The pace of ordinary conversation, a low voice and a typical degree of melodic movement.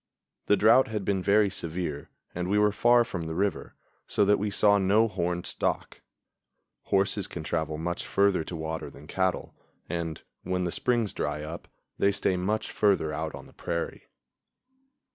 Yes: average, 170 wpm; very low, 95 Hz; average, 3.6 semitones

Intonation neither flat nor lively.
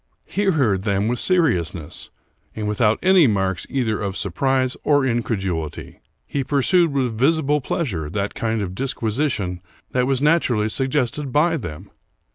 No: wide, 6.3 semitones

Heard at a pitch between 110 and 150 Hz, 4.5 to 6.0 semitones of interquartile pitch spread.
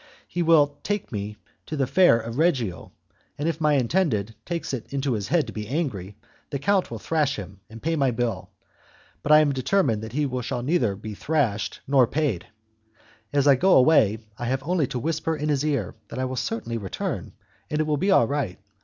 Yes: low, 135 Hz; average, 5.2 semitones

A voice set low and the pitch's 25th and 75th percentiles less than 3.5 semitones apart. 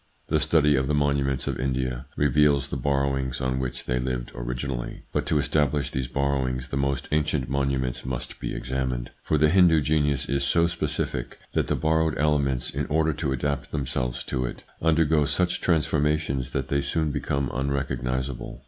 Yes: very low, 70 Hz; narrow, 2.5 semitones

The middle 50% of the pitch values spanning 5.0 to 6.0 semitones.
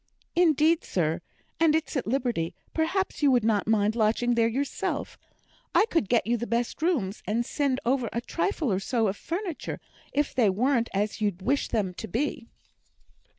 Yes: wide, 5.4 semitones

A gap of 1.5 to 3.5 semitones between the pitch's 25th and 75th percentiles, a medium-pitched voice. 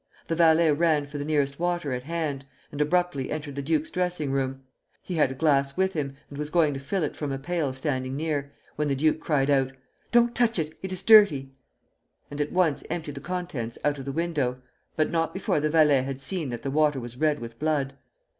Yes: average, 3.2 semitones; medium, 150 Hz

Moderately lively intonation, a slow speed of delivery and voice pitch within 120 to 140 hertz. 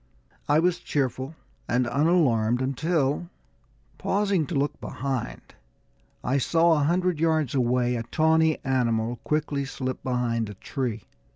Yes: average, 4.6 semitones; slow, 125 wpm; low, 135 Hz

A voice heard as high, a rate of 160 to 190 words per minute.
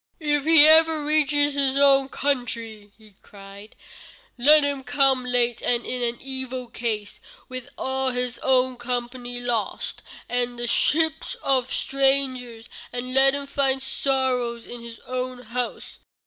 No: very high, 255 Hz; average, 145 wpm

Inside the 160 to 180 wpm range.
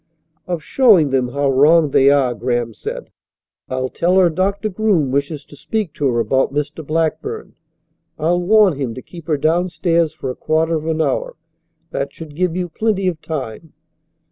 Yes: average, 175 wpm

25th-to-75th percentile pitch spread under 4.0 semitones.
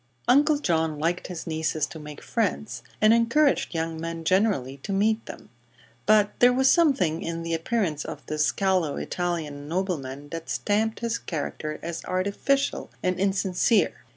No: average, 5.3 semitones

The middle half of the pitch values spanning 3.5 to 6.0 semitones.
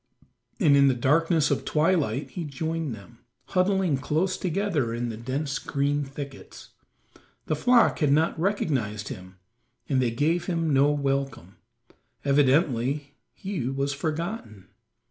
Yes: average, 3.8 semitones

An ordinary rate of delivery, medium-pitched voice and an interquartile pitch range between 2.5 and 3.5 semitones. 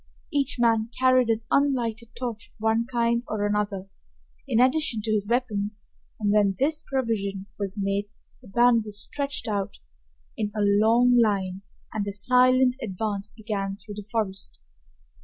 No: average, 155 wpm; high, 220 Hz; average, 3.2 semitones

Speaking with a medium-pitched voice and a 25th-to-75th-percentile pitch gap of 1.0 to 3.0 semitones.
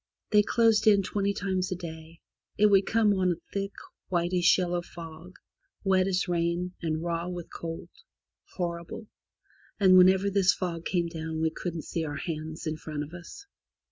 Yes: medium, 175 Hz; narrow, 2.6 semitones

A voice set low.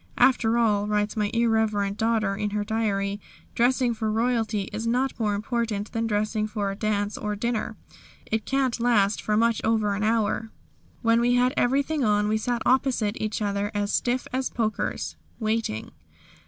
No: high, 220 Hz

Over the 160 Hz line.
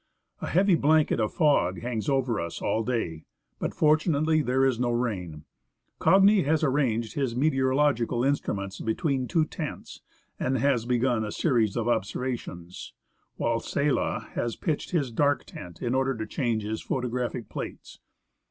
No: low, 125 Hz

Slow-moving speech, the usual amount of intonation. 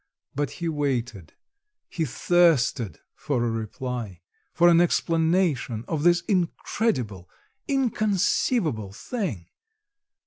No: slow, 95 wpm; wide, 6.9 semitones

